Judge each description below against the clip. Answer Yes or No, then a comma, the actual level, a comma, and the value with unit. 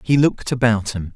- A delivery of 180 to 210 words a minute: Yes, fast, 205 wpm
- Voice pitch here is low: Yes, low, 115 Hz